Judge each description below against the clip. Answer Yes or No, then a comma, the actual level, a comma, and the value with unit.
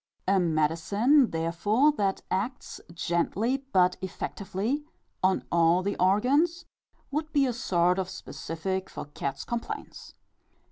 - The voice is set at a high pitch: Yes, high, 195 Hz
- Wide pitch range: Yes, wide, 6.4 semitones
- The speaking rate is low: Yes, slow, 120 wpm